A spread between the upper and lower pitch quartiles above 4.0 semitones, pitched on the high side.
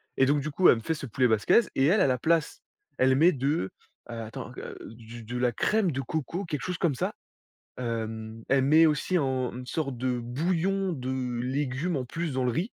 No: average, 4.8 semitones; low, 135 Hz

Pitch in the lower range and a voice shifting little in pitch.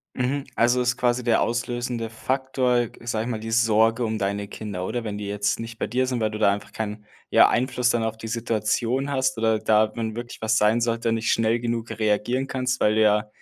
Yes: low, 115 Hz; narrow, 2.0 semitones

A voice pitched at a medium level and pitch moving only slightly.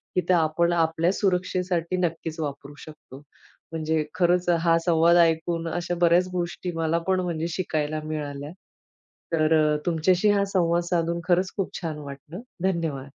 Yes: medium, 170 Hz; narrow, 2.2 semitones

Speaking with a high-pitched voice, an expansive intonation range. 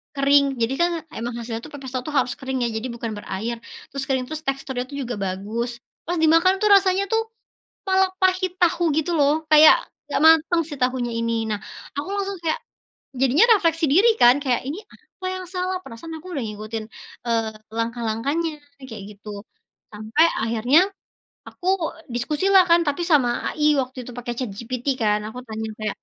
Yes: very high, 265 Hz; wide, 6.1 semitones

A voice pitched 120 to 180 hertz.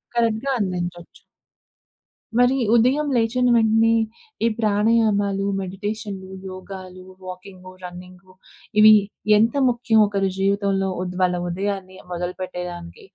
No: high, 195 Hz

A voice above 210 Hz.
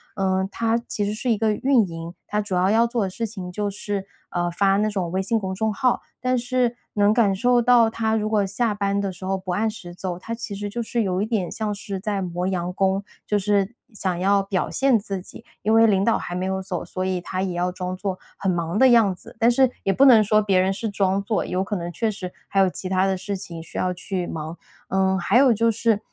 No: high, 200 Hz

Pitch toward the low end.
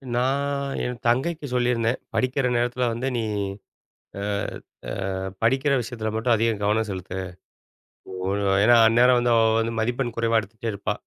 Yes: low, 120 Hz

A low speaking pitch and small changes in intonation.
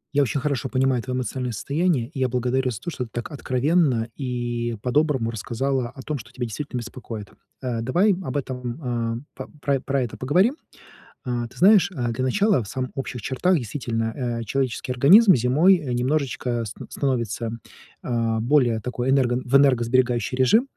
No: low, 130 Hz; average, 3.0 semitones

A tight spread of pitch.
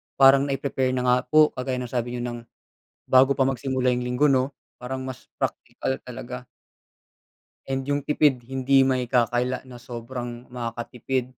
Yes: narrow, 1.5 semitones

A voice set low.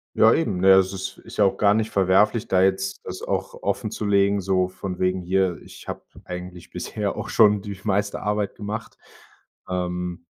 Yes: very low, 95 Hz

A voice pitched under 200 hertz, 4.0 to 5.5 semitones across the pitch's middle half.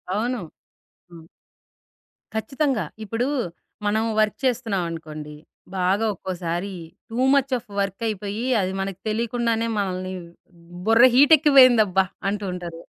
No: high, 210 Hz; average, 4.3 semitones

